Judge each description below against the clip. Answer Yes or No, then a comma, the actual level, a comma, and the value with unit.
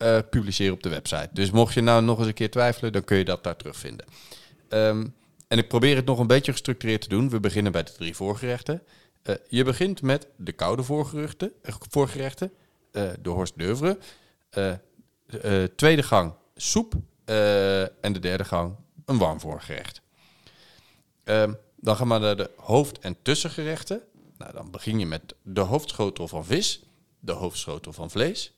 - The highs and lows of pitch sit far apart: Yes, wide, 5.9 semitones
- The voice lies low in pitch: Yes, low, 115 Hz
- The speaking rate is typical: Yes, average, 180 wpm